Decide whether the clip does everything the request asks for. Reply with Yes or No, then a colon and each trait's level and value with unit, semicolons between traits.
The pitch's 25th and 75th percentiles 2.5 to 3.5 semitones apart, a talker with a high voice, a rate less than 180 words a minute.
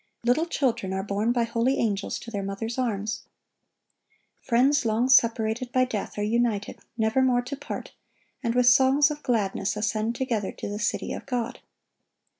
Yes: average, 3.1 semitones; high, 235 Hz; average, 160 wpm